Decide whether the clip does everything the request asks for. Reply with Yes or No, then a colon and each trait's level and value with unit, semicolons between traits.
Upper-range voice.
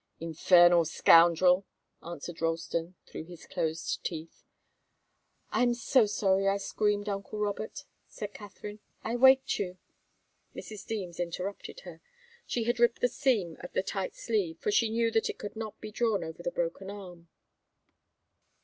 Yes: high, 195 Hz